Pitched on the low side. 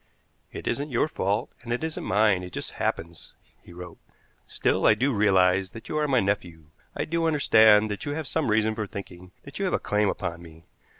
Yes: low, 105 Hz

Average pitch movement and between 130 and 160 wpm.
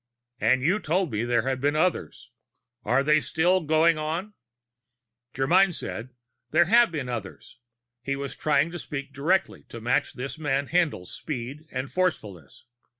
Yes: average, 4.7 semitones; average, 150 wpm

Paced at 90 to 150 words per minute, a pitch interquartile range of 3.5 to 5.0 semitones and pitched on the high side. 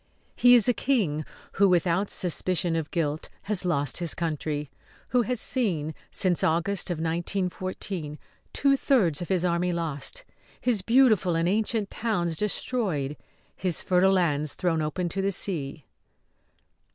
No: average, 140 wpm; average, 4.0 semitones; medium, 180 Hz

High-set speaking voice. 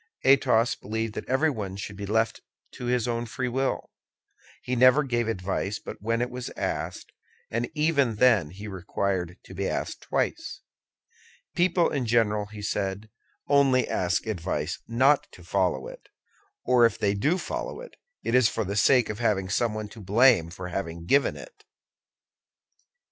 No: low, 115 Hz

